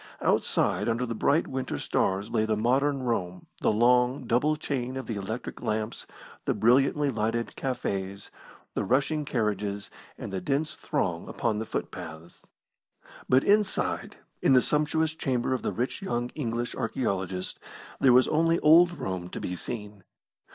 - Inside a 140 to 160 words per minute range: Yes, average, 150 wpm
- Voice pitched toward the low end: Yes, low, 120 Hz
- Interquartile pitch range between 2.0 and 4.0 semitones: No, average, 4.5 semitones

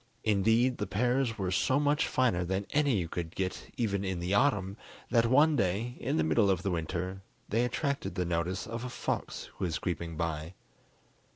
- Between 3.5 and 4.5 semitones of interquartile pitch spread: No, wide, 5.6 semitones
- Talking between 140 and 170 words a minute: No, average, 190 wpm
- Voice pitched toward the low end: Yes, low, 100 Hz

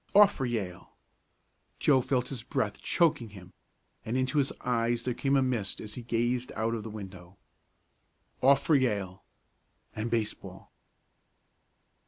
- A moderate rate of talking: Yes, average, 145 wpm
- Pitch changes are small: No, average, 3.5 semitones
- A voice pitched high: No, low, 120 Hz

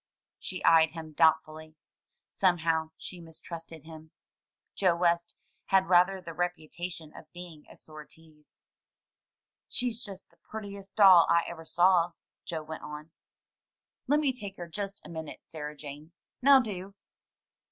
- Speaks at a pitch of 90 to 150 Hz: No, medium, 170 Hz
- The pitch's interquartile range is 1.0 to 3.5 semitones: Yes, average, 3.2 semitones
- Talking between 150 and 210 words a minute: No, slow, 135 wpm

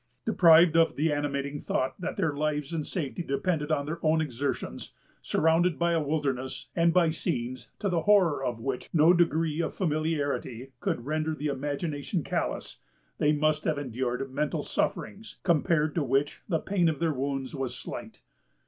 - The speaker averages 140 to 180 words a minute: Yes, average, 165 wpm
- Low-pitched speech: No, medium, 150 Hz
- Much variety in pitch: No, average, 2.9 semitones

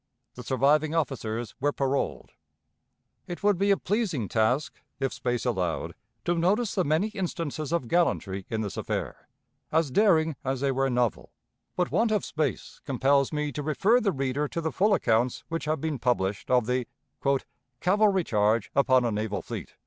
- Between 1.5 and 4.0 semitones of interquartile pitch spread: No, wide, 5.6 semitones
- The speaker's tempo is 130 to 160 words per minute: No, average, 170 wpm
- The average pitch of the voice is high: No, medium, 140 Hz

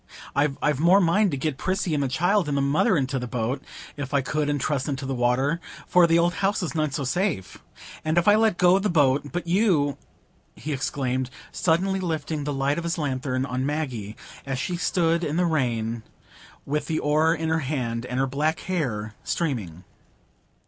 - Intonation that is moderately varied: Yes, average, 4.2 semitones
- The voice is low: No, medium, 150 Hz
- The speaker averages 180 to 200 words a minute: Yes, average, 190 wpm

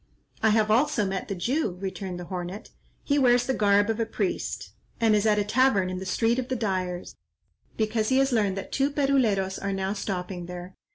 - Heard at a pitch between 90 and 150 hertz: No, high, 210 Hz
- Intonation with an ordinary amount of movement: Yes, average, 4.0 semitones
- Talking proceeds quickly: Yes, fast, 210 wpm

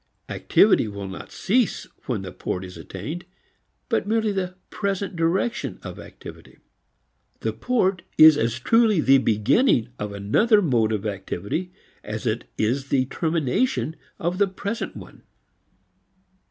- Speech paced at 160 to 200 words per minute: No, slow, 135 wpm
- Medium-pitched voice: Yes, medium, 160 Hz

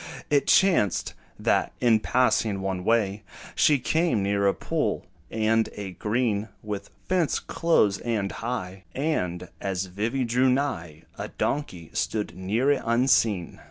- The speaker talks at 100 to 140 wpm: Yes, slow, 135 wpm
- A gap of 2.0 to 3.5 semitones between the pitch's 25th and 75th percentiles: No, average, 4.6 semitones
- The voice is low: Yes, low, 110 Hz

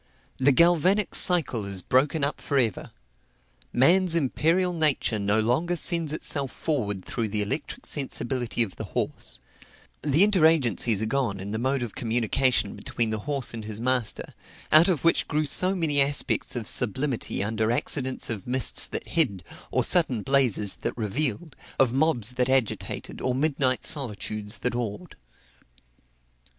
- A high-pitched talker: No, low, 130 Hz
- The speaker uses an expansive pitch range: Yes, wide, 5.7 semitones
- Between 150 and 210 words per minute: Yes, average, 155 wpm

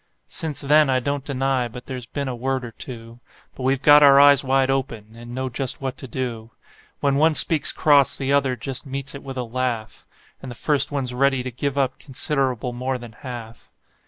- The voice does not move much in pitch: Yes, narrow, 2.0 semitones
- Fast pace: Yes, fast, 210 wpm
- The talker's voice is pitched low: Yes, low, 130 Hz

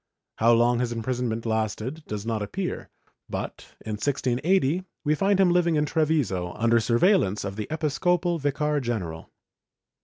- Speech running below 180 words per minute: Yes, average, 145 wpm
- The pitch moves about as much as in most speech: No, wide, 6.4 semitones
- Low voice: Yes, low, 125 Hz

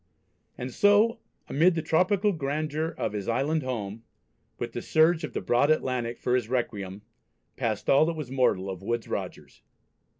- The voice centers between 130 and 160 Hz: Yes, low, 135 Hz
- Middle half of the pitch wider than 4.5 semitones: Yes, wide, 5.4 semitones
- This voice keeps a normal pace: Yes, average, 165 wpm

